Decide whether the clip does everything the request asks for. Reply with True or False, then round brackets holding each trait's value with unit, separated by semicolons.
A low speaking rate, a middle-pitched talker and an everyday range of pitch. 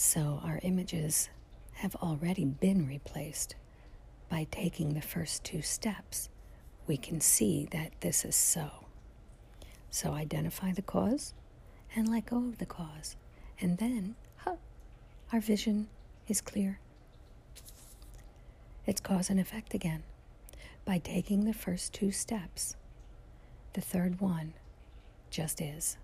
True (120 wpm; 180 Hz; 4.4 semitones)